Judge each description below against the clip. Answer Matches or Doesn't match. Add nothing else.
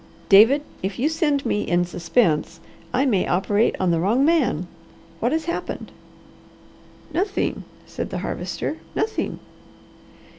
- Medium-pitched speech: Doesn't match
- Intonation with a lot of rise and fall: Matches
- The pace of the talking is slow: Matches